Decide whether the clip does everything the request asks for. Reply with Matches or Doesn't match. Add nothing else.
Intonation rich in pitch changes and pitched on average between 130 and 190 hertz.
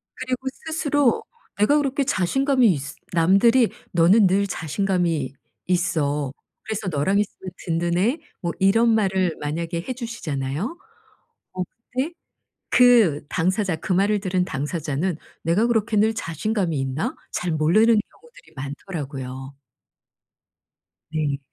Matches